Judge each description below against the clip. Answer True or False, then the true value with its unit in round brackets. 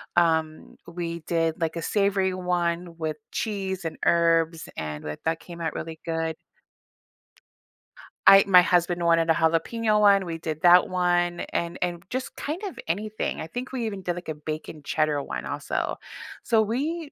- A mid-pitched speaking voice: True (170 Hz)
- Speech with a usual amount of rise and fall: True (3.2 semitones)